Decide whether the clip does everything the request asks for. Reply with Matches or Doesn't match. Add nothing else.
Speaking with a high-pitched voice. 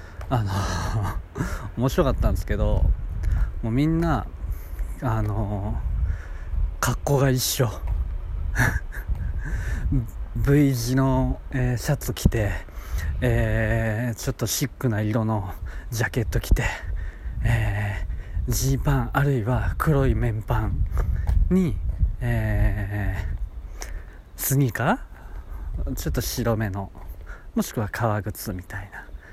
Doesn't match